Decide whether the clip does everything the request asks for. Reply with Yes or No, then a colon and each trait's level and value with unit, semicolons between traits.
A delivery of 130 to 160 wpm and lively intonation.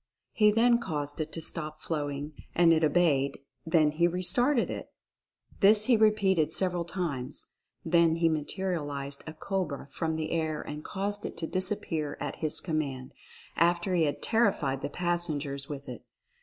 No: average, 155 wpm; average, 3.8 semitones